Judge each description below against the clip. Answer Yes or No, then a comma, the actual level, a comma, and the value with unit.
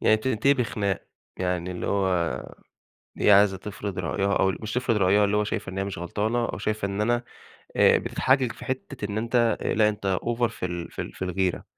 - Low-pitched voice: Yes, low, 105 Hz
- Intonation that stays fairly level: No, average, 3.2 semitones